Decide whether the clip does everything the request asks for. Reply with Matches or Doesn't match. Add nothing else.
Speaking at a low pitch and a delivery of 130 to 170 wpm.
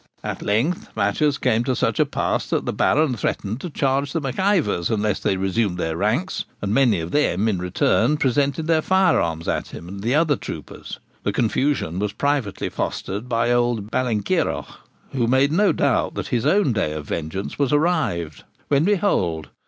Doesn't match